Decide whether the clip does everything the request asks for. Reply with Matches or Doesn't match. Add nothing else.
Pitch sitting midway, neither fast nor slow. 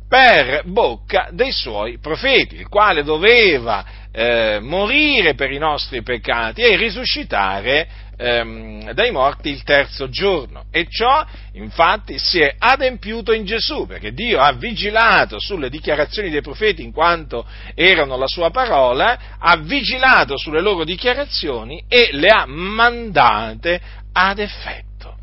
Matches